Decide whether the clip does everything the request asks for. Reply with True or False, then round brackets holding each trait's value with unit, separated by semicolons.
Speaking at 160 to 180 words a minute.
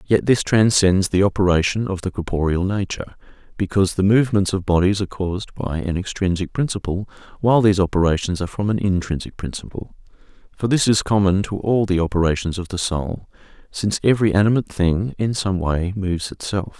True (170 wpm)